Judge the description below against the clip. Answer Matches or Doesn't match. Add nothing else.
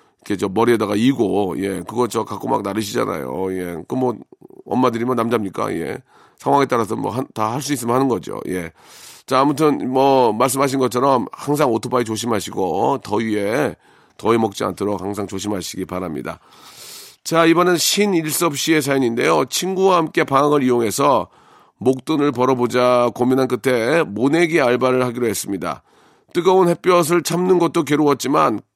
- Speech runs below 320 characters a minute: Doesn't match